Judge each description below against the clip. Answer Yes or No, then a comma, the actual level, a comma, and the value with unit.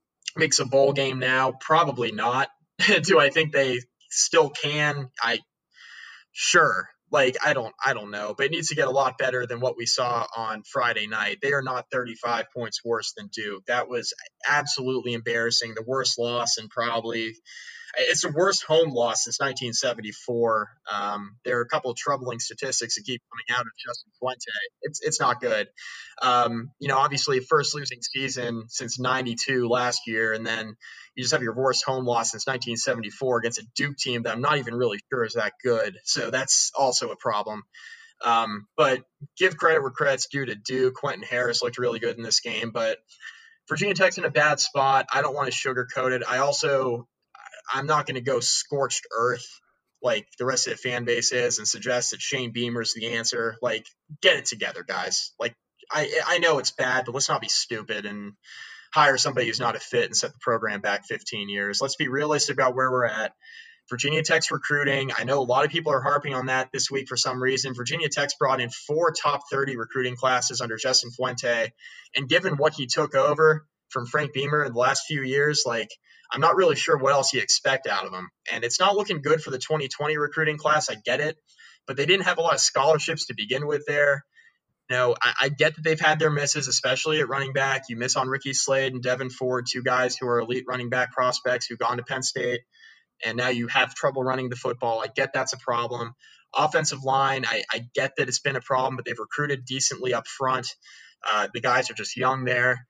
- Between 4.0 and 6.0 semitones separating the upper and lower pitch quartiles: No, average, 3.4 semitones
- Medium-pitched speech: No, low, 130 Hz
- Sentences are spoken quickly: Yes, fast, 210 wpm